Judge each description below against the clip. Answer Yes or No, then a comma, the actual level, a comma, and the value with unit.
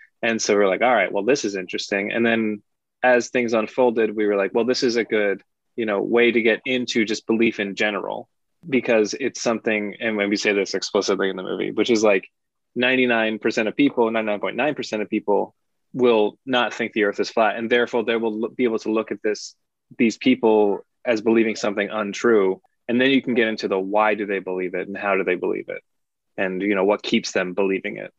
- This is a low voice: Yes, low, 110 Hz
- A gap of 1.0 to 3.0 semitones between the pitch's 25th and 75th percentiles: Yes, narrow, 2.4 semitones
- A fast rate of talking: Yes, fast, 220 wpm